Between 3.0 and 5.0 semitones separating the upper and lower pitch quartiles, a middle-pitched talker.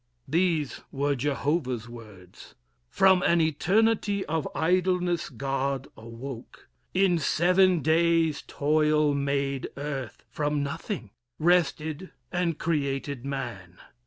Yes: average, 4.0 semitones; medium, 150 Hz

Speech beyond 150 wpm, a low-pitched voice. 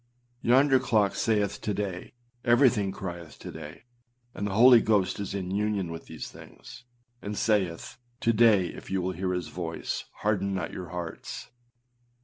Yes: average, 160 wpm; low, 100 Hz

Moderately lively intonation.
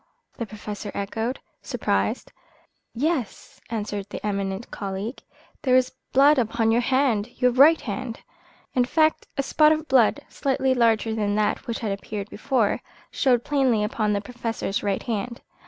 Yes: average, 3.9 semitones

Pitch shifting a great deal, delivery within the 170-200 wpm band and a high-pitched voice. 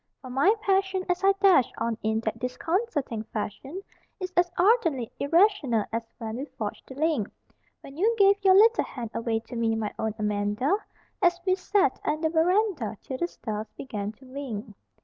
Yes: wide, 9.0 semitones; average, 180 wpm; very high, 275 Hz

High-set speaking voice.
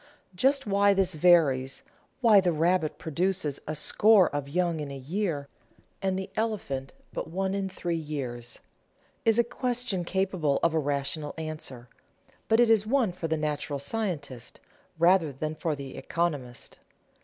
No: medium, 170 Hz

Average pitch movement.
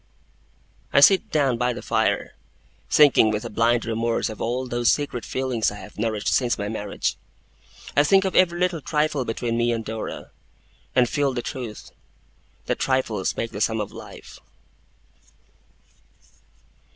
Yes: average, 3.8 semitones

